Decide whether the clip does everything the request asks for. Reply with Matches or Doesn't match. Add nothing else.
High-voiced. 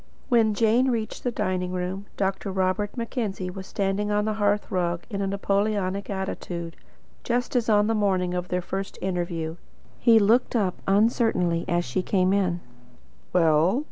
Matches